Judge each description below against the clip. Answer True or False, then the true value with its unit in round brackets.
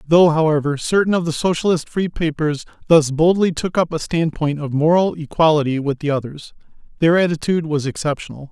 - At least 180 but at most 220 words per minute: False (170 wpm)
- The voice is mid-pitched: True (160 Hz)